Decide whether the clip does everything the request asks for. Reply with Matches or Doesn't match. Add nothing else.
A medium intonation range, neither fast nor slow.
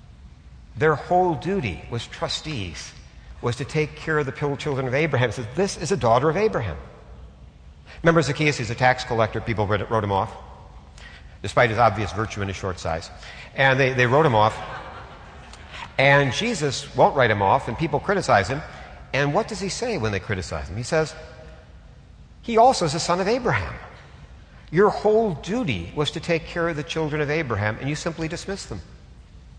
Doesn't match